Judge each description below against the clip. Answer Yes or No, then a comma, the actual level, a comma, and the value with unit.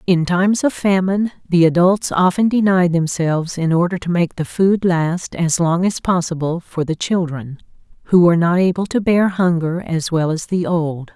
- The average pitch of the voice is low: No, medium, 175 Hz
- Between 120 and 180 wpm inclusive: No, average, 190 wpm